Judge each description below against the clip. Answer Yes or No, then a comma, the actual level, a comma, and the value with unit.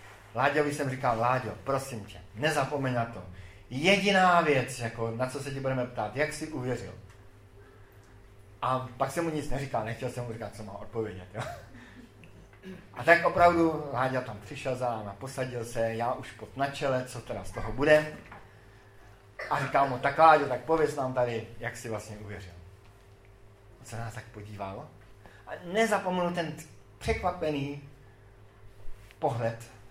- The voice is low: Yes, low, 115 Hz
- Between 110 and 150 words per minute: No, average, 160 wpm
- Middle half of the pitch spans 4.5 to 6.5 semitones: Yes, wide, 5.5 semitones